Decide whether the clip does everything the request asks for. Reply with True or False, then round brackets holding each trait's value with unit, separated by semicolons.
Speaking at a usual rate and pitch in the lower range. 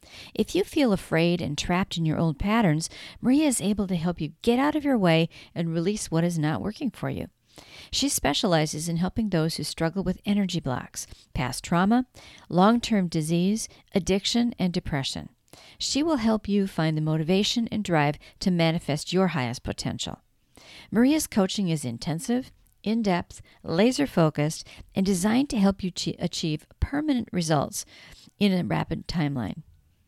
False (160 wpm; 185 Hz)